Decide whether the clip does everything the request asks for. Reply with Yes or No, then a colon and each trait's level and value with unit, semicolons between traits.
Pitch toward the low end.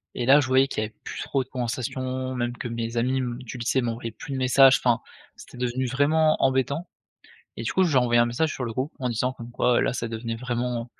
Yes: low, 125 Hz